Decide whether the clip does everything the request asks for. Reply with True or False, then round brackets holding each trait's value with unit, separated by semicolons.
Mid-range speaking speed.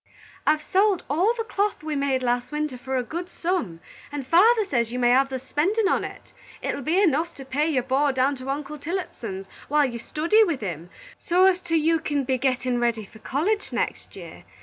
False (210 wpm)